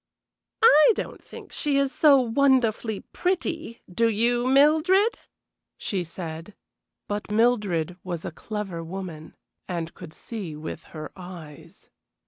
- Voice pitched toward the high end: Yes, high, 210 Hz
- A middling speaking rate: No, slow, 120 wpm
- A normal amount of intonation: No, wide, 7.7 semitones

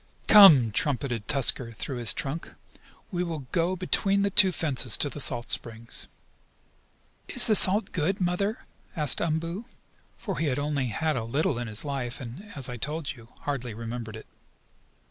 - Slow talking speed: No, average, 165 wpm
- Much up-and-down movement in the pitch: Yes, wide, 6.3 semitones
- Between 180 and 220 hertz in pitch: No, medium, 145 Hz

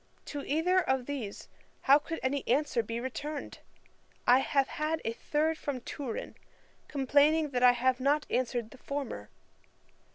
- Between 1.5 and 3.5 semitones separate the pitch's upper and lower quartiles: Yes, average, 3.1 semitones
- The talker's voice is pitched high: Yes, very high, 275 Hz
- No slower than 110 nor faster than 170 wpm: Yes, average, 150 wpm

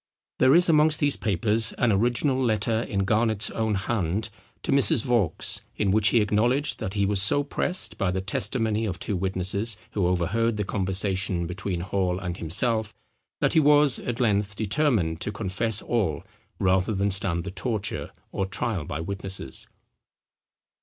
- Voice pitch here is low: Yes, low, 105 Hz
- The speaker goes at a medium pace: Yes, average, 160 wpm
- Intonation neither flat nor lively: Yes, average, 3.5 semitones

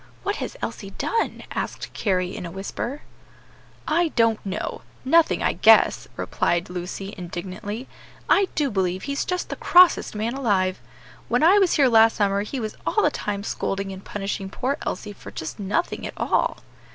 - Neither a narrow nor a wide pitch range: No, wide, 6.5 semitones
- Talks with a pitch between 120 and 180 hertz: No, high, 210 Hz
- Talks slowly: No, average, 170 wpm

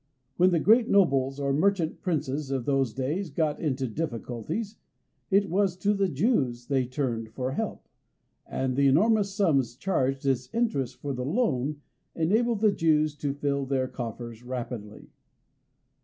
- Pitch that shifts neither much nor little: No, wide, 6.3 semitones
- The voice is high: No, medium, 140 Hz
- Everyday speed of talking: Yes, average, 150 wpm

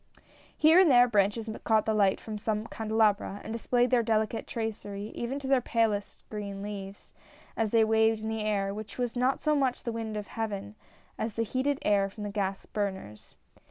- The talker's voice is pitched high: Yes, high, 220 Hz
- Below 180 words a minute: No, average, 195 wpm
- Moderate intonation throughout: No, narrow, 2.2 semitones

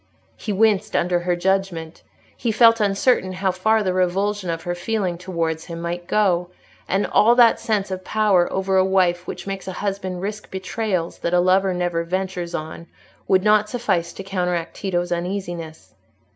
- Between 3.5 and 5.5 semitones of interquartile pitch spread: No, narrow, 2.6 semitones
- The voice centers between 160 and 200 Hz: Yes, medium, 185 Hz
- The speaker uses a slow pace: No, average, 170 wpm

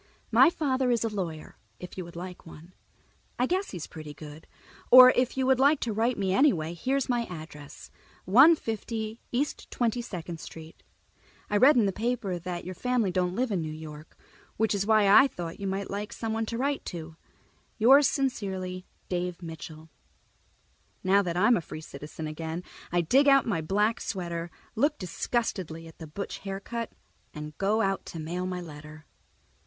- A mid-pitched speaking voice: No, high, 195 Hz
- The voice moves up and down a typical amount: No, wide, 6.0 semitones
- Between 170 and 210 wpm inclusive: Yes, average, 175 wpm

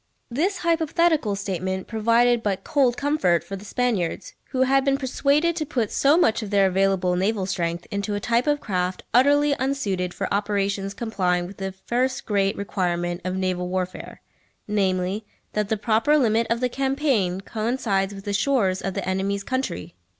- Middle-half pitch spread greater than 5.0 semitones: Yes, wide, 5.4 semitones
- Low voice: No, high, 205 Hz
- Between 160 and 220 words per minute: Yes, average, 170 wpm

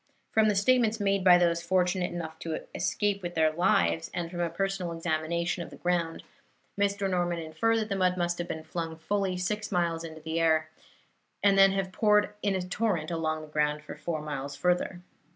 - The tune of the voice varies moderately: Yes, average, 3.3 semitones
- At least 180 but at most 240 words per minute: Yes, average, 200 wpm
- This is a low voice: No, medium, 175 Hz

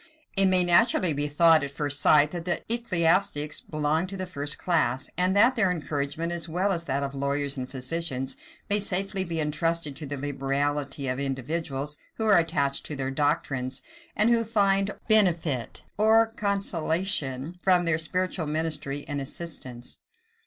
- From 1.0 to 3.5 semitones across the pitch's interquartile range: No, average, 4.7 semitones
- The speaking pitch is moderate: Yes, medium, 160 Hz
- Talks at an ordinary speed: Yes, average, 160 wpm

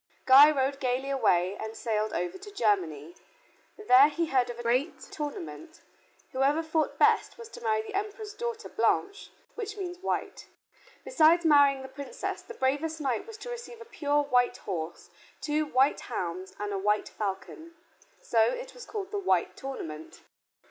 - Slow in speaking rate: No, average, 165 wpm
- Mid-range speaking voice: No, very high, 285 Hz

